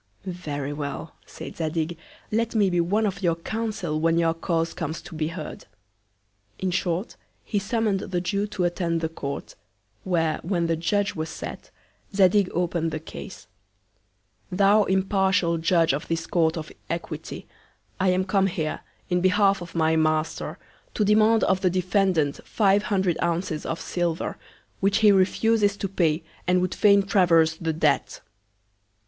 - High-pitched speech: No, medium, 180 Hz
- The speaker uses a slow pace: No, average, 155 wpm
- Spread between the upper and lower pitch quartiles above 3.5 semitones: No, average, 3.1 semitones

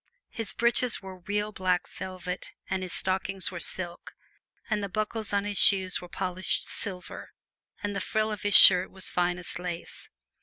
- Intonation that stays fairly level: Yes, narrow, 2.2 semitones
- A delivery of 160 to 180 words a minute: Yes, average, 165 wpm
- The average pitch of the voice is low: No, high, 190 Hz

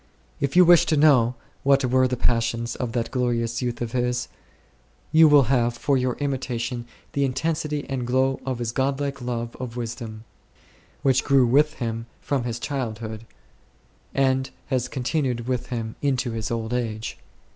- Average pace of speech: Yes, average, 165 wpm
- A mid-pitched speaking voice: No, low, 125 Hz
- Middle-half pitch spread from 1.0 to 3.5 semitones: Yes, narrow, 2.6 semitones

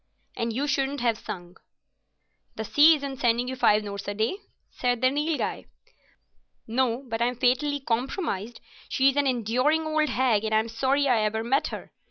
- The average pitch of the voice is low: No, very high, 250 Hz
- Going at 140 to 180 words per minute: Yes, average, 170 wpm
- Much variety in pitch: No, average, 3.7 semitones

